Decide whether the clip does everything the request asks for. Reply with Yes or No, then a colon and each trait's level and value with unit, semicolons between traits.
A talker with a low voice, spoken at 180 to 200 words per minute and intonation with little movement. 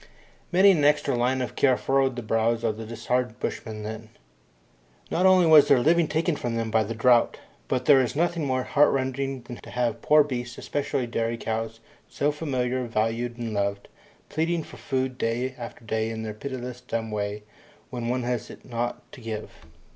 No: low, 125 Hz; average, 185 wpm; average, 3.3 semitones